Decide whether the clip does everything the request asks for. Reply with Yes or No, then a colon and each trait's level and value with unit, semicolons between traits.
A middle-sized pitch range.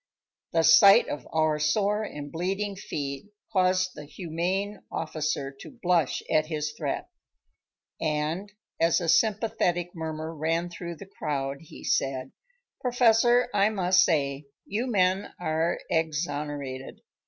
Yes: average, 4.1 semitones